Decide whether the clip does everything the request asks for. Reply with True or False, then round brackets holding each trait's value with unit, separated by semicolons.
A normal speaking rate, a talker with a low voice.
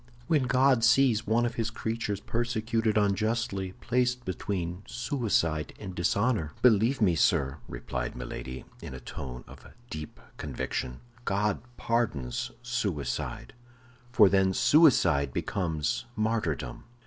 False (115 wpm; 105 Hz)